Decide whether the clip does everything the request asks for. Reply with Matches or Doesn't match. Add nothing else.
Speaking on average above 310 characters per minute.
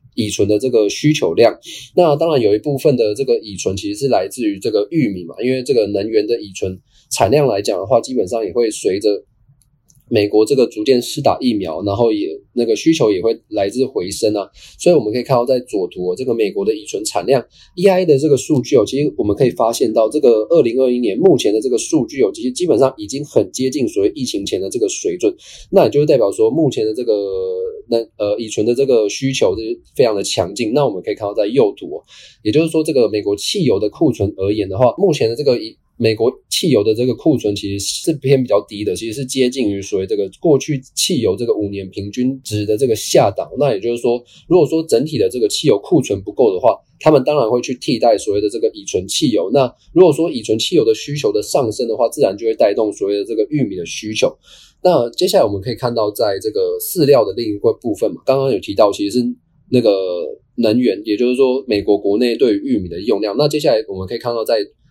Matches